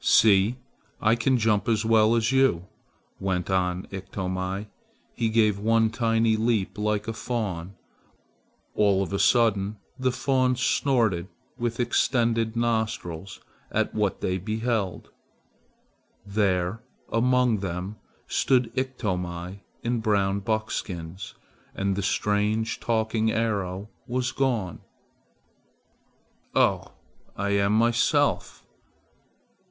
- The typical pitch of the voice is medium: No, low, 110 Hz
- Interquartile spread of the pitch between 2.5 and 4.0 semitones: Yes, average, 3.1 semitones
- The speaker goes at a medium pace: No, slow, 105 wpm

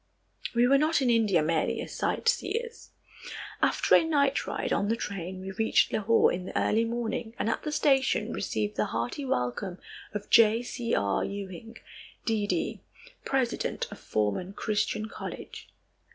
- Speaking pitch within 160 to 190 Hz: No, high, 220 Hz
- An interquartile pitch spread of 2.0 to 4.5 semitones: No, average, 5.1 semitones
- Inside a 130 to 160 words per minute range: Yes, average, 150 wpm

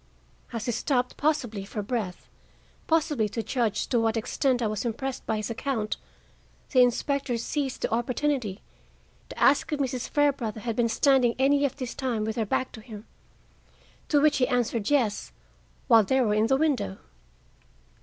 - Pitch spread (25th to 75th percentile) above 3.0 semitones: Yes, average, 3.7 semitones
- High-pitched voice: Yes, high, 245 Hz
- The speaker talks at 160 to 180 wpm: Yes, average, 170 wpm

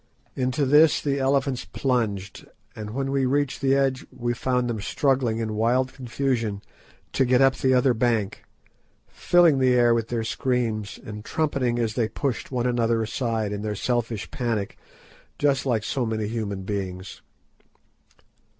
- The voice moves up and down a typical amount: Yes, average, 3.3 semitones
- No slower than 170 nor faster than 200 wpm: No, average, 155 wpm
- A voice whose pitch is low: Yes, low, 120 Hz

